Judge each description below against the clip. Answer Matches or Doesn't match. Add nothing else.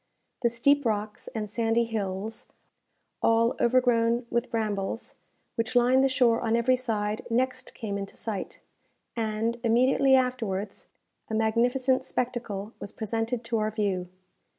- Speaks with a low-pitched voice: Doesn't match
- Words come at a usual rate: Doesn't match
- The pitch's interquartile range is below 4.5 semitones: Matches